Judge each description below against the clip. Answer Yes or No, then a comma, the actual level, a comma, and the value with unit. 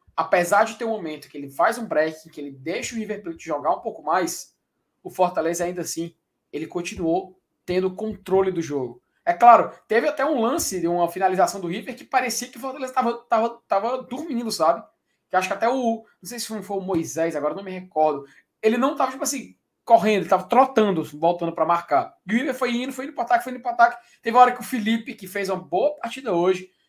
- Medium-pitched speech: No, high, 205 Hz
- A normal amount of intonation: No, wide, 6.3 semitones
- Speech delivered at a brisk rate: Yes, fast, 230 wpm